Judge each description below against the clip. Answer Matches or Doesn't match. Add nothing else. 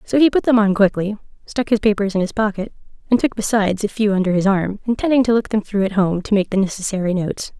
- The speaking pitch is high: Matches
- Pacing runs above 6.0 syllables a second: Matches